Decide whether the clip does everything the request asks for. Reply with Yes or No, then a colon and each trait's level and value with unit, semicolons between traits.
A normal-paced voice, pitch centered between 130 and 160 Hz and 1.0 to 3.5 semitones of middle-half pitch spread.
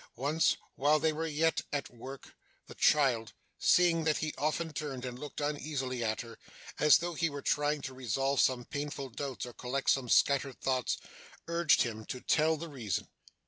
Yes: average, 180 wpm; medium, 140 Hz; average, 3.1 semitones